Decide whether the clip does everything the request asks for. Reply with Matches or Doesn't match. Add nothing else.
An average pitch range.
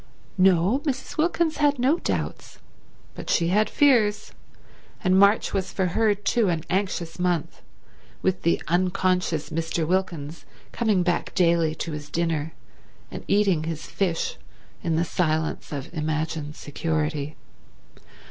Matches